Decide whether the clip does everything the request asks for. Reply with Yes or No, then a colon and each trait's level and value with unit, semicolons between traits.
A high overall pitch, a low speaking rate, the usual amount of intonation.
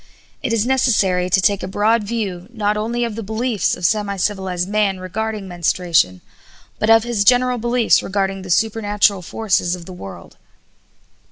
No: high, 205 Hz; average, 165 wpm; average, 3.3 semitones